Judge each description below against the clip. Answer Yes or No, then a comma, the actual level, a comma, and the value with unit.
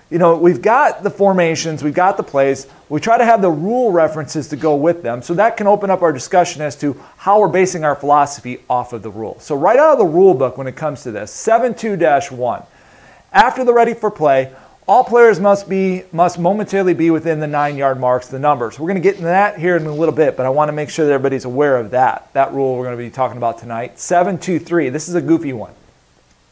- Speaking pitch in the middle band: Yes, medium, 160 Hz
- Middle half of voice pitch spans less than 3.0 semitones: No, wide, 5.6 semitones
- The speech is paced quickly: Yes, fast, 255 wpm